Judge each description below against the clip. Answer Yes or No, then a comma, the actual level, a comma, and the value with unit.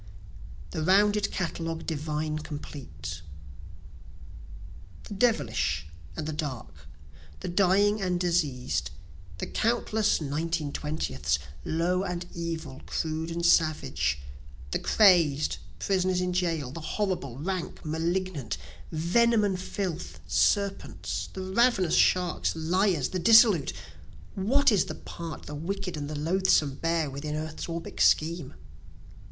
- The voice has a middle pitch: Yes, medium, 165 Hz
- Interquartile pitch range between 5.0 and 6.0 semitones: No, average, 3.9 semitones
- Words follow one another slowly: Yes, slow, 115 wpm